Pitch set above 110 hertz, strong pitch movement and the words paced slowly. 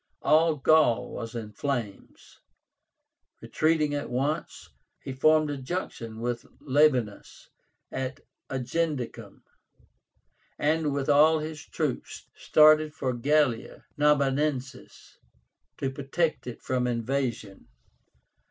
No: medium, 140 Hz; average, 3.8 semitones; slow, 95 wpm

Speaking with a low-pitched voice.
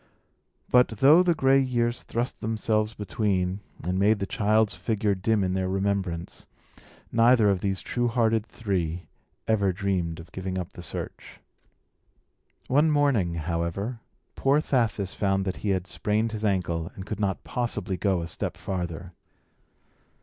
Yes: low, 100 Hz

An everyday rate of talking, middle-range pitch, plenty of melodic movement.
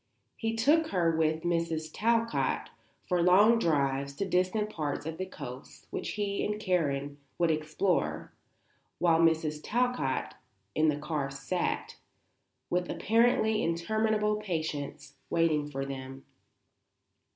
No: slow, 120 wpm; medium, 165 Hz; wide, 6.0 semitones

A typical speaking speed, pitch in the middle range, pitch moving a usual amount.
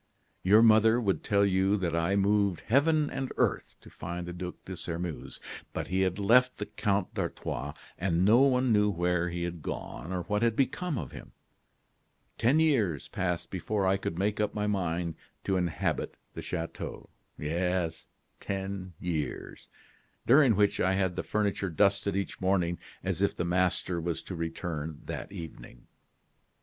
No: average, 165 wpm; very low, 95 Hz; average, 3.1 semitones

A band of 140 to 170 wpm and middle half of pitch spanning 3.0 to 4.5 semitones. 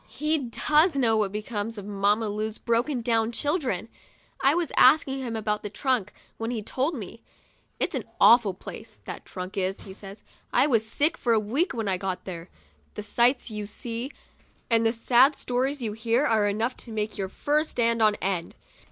No: average, 195 wpm; average, 3.6 semitones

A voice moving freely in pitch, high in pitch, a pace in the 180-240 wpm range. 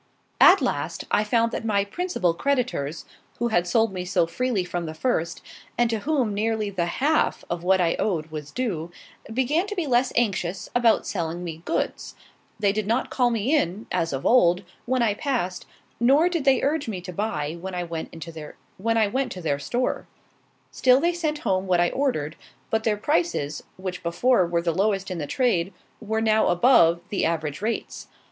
Yes: wide, 6.2 semitones; high, 205 Hz; average, 185 wpm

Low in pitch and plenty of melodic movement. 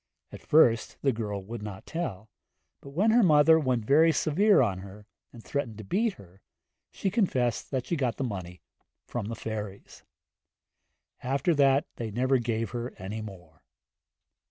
Yes: low, 120 Hz; wide, 5.8 semitones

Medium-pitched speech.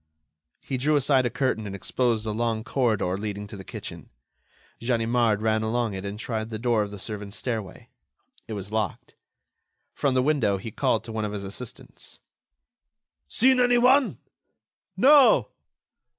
No: low, 110 Hz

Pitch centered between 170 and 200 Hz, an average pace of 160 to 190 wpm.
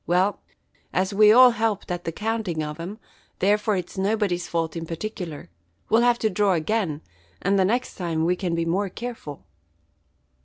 Yes: high, 190 Hz; average, 170 wpm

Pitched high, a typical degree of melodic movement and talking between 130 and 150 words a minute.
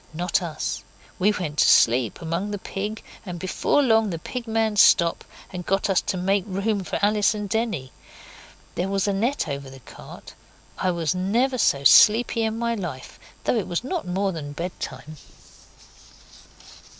No: high, 195 Hz; average, 4.4 semitones; average, 170 wpm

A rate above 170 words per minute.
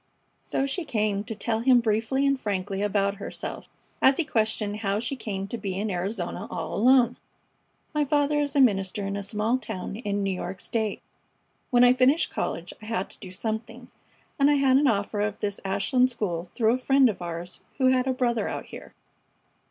Yes: average, 200 wpm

